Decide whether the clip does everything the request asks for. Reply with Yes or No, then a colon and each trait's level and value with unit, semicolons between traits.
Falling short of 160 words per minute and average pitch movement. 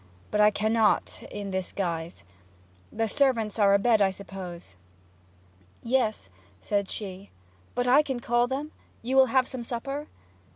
Yes: average, 140 wpm; average, 4.1 semitones